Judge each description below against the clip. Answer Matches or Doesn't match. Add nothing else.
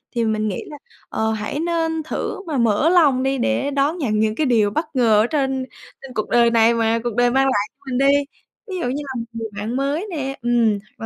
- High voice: Matches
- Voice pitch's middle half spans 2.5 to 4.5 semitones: Matches